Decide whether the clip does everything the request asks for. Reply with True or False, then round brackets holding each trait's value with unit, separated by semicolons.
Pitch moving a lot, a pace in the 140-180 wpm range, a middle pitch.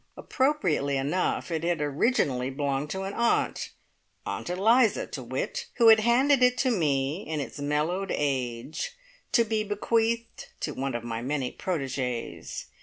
True (8.8 semitones; 150 wpm; 170 Hz)